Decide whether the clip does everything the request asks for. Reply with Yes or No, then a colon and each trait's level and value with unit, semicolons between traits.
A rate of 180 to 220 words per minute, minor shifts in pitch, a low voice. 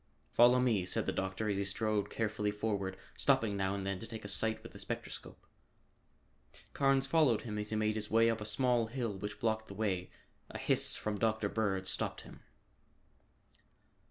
Yes: average, 185 wpm; narrow, 2.2 semitones; low, 110 Hz